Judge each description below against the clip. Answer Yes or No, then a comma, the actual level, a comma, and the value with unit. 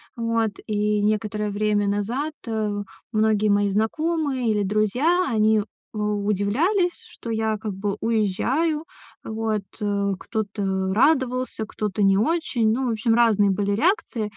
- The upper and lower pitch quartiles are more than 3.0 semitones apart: No, average, 2.7 semitones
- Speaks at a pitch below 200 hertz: No, high, 215 Hz